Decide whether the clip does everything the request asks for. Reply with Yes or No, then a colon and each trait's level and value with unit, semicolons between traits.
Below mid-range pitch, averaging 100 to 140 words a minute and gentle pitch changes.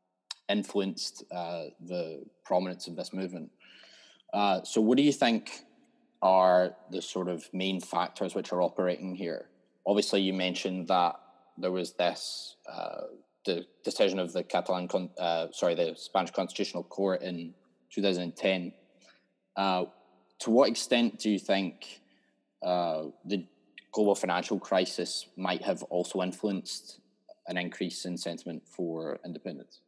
Yes: very low, 90 Hz; slow, 135 wpm; narrow, 1.5 semitones